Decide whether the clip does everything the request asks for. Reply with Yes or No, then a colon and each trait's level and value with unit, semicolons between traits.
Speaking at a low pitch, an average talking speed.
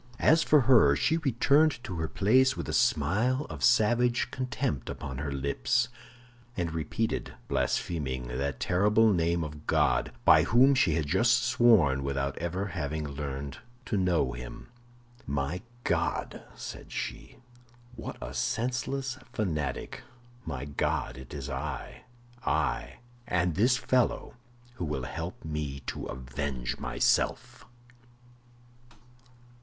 No: very low, 85 Hz; slow, 120 wpm